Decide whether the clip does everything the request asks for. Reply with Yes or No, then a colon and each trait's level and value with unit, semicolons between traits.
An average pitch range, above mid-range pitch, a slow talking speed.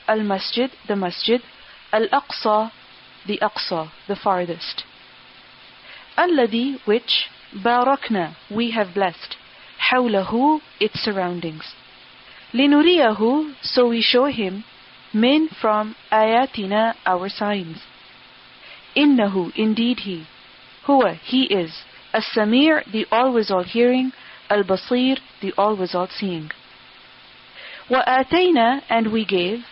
Yes: average, 4.4 semitones; high, 220 Hz; slow, 105 wpm